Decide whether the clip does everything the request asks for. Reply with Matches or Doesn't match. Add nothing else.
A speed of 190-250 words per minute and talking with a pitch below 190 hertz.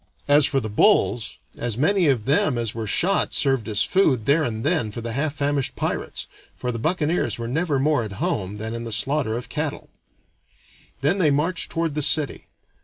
Matches